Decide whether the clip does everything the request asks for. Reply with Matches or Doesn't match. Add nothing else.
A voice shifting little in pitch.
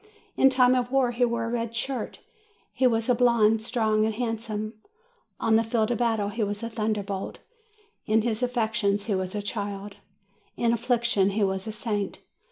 Matches